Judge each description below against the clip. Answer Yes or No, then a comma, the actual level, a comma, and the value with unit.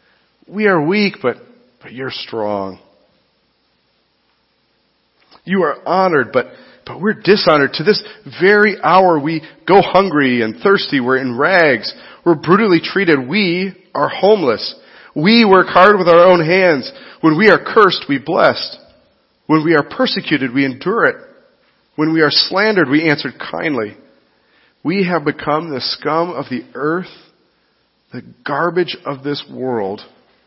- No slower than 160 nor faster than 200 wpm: No, average, 140 wpm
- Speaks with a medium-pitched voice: Yes, medium, 165 Hz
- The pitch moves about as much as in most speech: Yes, average, 5.0 semitones